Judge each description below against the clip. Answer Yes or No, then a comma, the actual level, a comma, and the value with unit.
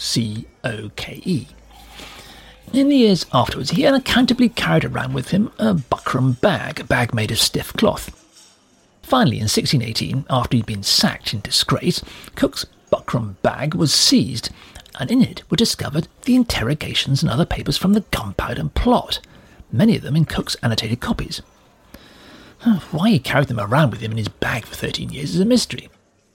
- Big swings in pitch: Yes, wide, 8.6 semitones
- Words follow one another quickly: No, average, 170 wpm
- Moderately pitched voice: Yes, medium, 145 Hz